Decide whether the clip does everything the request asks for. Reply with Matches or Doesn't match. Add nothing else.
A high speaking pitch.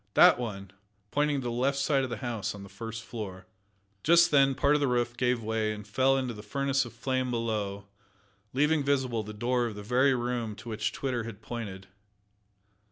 Doesn't match